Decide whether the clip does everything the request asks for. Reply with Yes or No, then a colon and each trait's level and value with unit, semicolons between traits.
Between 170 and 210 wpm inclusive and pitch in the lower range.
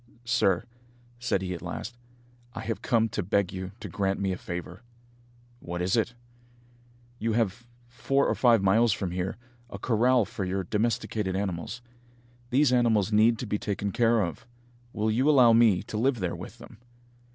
Yes: average, 175 wpm; low, 110 Hz